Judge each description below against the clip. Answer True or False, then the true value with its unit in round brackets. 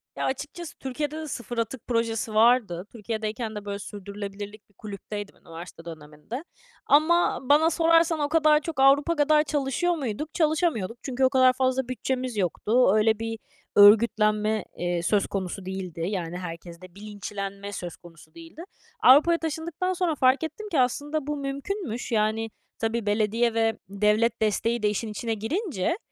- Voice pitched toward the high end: True (230 Hz)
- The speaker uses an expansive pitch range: True (6.2 semitones)